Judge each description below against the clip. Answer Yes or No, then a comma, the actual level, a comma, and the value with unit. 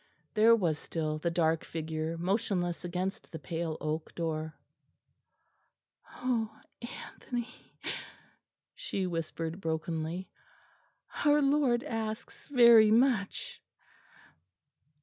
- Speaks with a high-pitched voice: No, medium, 180 Hz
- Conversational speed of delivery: No, slow, 90 wpm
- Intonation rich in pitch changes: Yes, wide, 6.2 semitones